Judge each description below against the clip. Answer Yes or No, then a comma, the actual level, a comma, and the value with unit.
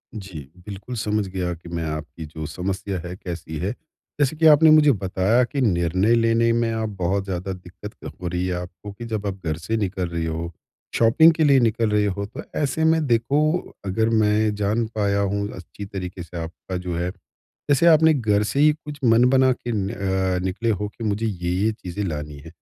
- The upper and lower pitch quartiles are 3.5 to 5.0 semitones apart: Yes, average, 4.3 semitones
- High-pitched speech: No, low, 100 Hz